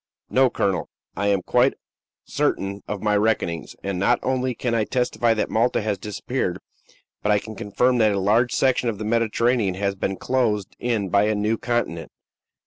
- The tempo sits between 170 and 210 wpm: Yes, average, 180 wpm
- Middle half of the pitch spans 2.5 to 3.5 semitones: Yes, average, 3.1 semitones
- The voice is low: Yes, low, 110 Hz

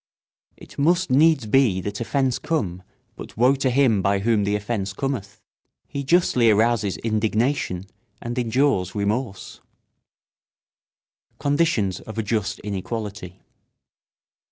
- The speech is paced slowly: Yes, slow, 120 wpm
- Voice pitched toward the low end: Yes, low, 110 Hz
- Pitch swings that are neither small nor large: Yes, average, 4.9 semitones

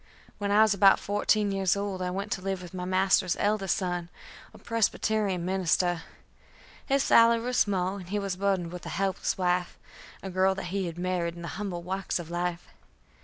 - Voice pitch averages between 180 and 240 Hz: Yes, high, 190 Hz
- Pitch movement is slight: Yes, narrow, 2.0 semitones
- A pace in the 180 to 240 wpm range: Yes, average, 195 wpm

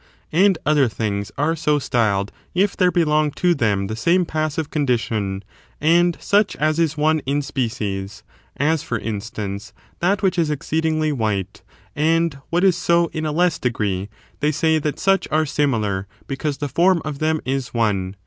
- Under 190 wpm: Yes, average, 170 wpm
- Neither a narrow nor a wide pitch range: No, wide, 6.7 semitones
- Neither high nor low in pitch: Yes, medium, 150 Hz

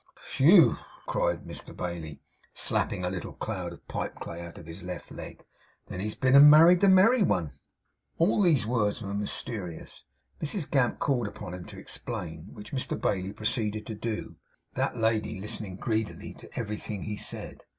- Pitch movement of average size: No, wide, 6.2 semitones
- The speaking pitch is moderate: No, low, 105 Hz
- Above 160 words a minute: Yes, average, 170 wpm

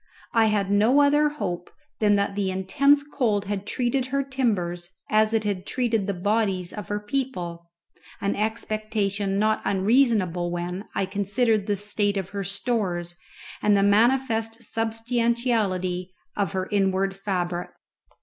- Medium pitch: No, high, 205 Hz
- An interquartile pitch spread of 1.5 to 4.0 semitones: Yes, average, 3.1 semitones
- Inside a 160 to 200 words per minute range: No, average, 140 wpm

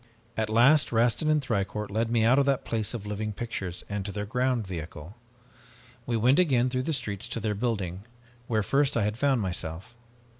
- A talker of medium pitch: No, low, 115 Hz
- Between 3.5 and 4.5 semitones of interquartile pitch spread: Yes, average, 3.8 semitones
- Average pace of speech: Yes, average, 195 wpm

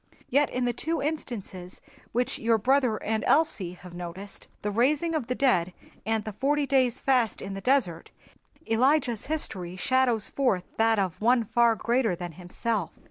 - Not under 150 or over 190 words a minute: Yes, average, 165 wpm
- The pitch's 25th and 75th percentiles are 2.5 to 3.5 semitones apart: No, average, 5.2 semitones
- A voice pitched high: Yes, high, 230 Hz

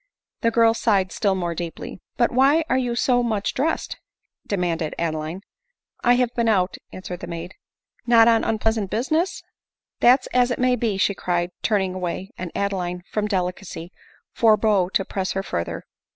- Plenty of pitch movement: No, average, 4.6 semitones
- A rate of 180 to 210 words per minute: Yes, average, 185 wpm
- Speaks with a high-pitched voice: Yes, high, 200 Hz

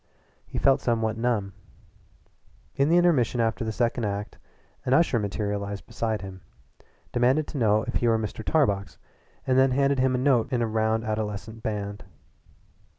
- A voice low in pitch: Yes, low, 115 Hz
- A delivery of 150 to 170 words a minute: Yes, average, 165 wpm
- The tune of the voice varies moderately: Yes, average, 3.5 semitones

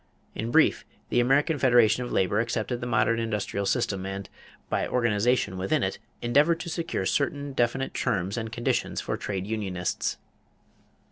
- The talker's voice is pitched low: Yes, low, 115 Hz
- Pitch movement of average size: Yes, average, 3.8 semitones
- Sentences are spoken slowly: No, average, 150 wpm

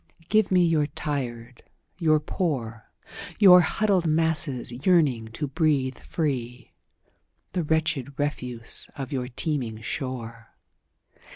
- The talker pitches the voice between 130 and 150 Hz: Yes, medium, 140 Hz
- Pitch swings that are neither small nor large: Yes, average, 4.8 semitones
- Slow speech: Yes, slow, 95 wpm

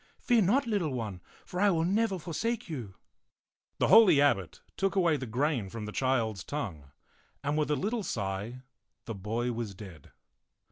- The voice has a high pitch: No, medium, 140 Hz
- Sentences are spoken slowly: No, average, 175 wpm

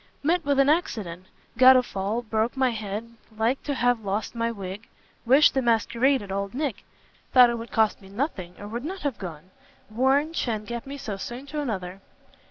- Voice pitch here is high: Yes, high, 235 Hz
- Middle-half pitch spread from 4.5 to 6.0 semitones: Yes, average, 4.8 semitones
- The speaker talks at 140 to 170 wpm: No, average, 190 wpm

